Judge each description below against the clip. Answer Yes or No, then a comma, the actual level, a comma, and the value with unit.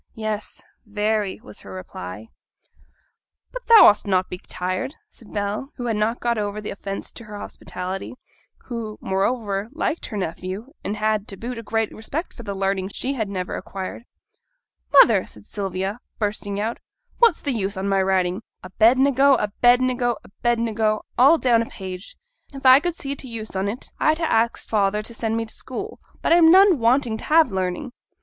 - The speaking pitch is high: Yes, high, 215 Hz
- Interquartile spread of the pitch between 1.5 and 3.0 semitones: No, average, 4.1 semitones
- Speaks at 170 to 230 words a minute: Yes, average, 185 wpm